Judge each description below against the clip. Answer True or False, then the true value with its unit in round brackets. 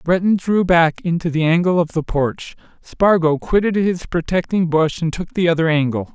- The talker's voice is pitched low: False (170 Hz)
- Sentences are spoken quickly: False (185 wpm)